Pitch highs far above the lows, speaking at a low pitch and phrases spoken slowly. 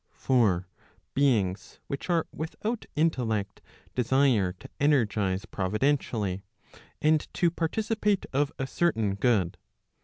Yes: wide, 7.4 semitones; low, 130 Hz; slow, 100 wpm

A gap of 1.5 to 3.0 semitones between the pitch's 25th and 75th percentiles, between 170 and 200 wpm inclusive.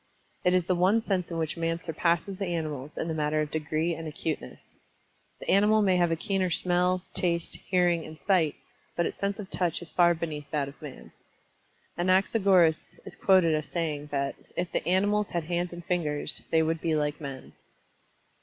Yes: average, 2.7 semitones; average, 190 wpm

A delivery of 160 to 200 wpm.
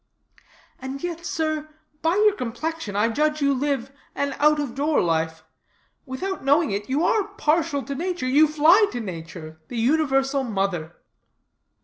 No: average, 150 wpm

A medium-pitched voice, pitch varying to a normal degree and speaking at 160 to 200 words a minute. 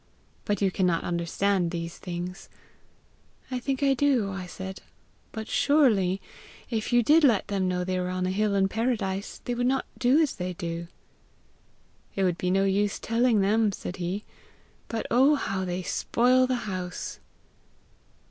No: high, 195 Hz; average, 4.8 semitones; average, 165 wpm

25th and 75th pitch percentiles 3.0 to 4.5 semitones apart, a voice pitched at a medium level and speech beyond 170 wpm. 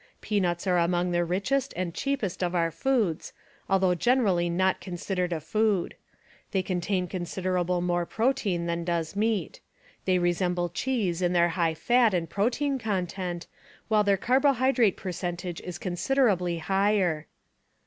No: average, 3.4 semitones; medium, 180 Hz; average, 140 wpm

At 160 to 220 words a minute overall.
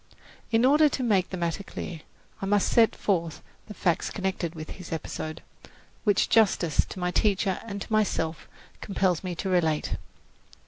Yes: average, 165 wpm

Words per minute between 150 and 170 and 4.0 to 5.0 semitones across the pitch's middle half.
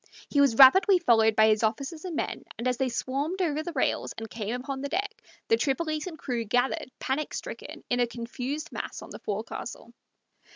No: average, 195 wpm; average, 4.7 semitones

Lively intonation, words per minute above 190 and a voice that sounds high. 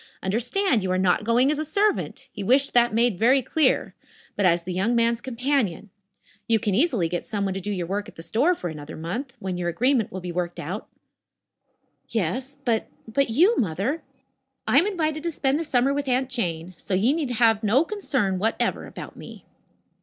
Yes: wide, 6.5 semitones; average, 200 wpm; high, 230 Hz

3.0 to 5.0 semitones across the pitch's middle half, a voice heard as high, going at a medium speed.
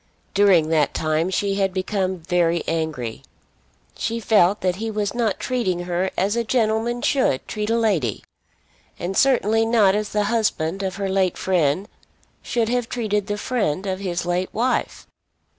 Yes: average, 3.9 semitones; high, 195 Hz; average, 160 wpm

